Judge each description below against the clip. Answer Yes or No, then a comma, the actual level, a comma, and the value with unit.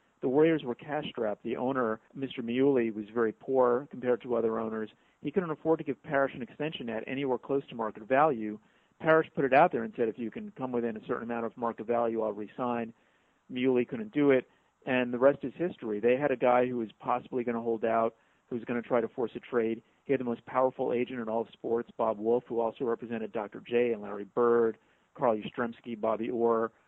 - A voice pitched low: Yes, low, 120 Hz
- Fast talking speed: Yes, fast, 230 wpm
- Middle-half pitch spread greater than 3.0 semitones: No, average, 2.7 semitones